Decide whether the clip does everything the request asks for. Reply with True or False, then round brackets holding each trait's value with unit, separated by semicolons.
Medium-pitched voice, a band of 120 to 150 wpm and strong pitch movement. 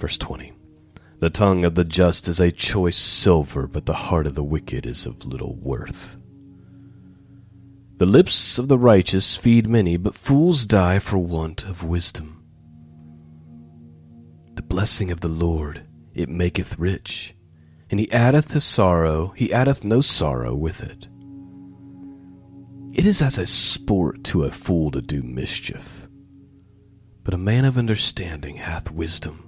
False (95 Hz; 145 wpm; 6.1 semitones)